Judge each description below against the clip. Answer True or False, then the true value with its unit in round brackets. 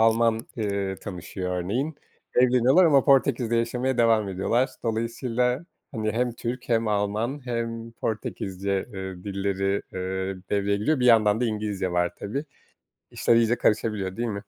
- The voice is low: True (110 Hz)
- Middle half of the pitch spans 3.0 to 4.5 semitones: True (3.5 semitones)